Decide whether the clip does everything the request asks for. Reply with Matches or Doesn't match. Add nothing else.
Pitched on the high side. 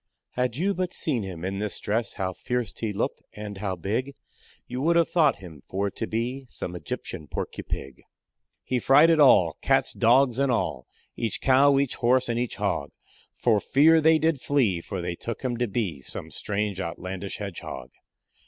Doesn't match